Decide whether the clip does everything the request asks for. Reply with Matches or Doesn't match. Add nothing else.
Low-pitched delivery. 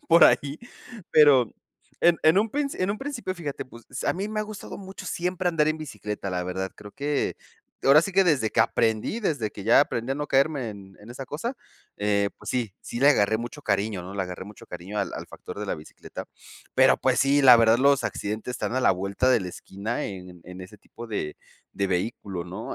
Matches